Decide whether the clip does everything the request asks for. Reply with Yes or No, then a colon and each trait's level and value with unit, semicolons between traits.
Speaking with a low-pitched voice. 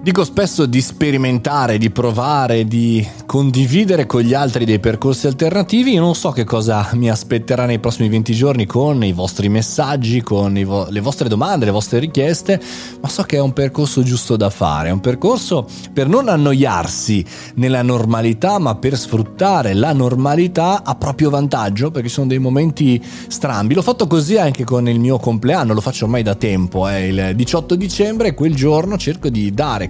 Yes: low, 130 Hz